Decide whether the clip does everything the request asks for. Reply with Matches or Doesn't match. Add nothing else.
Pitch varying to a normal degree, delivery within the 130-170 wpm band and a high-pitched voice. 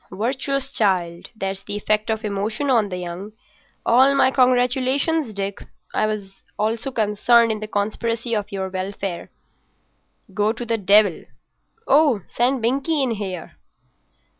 Matches